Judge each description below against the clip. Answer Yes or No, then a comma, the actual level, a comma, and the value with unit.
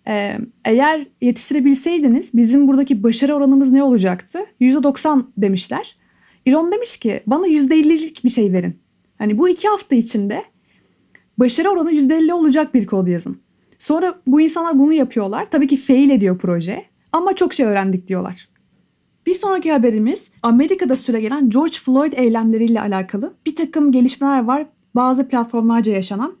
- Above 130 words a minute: Yes, fast, 140 wpm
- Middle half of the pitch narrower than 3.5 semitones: No, average, 5.1 semitones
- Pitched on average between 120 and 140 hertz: No, very high, 265 Hz